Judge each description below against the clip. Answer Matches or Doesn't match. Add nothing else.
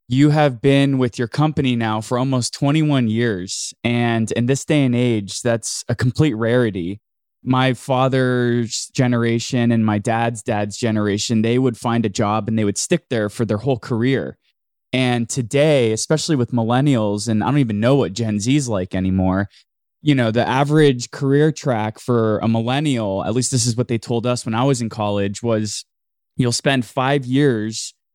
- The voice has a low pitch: Matches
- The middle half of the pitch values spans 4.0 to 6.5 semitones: Doesn't match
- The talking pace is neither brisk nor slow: Matches